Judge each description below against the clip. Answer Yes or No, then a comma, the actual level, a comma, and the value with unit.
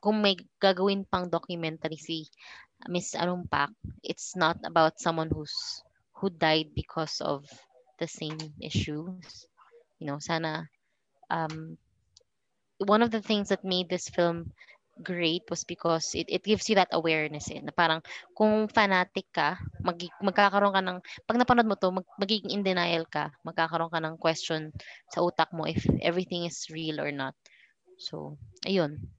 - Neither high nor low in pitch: Yes, medium, 170 Hz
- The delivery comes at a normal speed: Yes, average, 155 wpm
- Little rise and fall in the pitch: No, average, 3.4 semitones